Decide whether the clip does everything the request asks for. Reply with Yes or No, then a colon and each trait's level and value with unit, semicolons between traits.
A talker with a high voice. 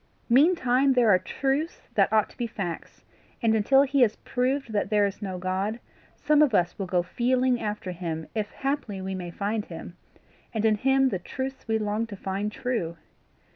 Yes: high, 220 Hz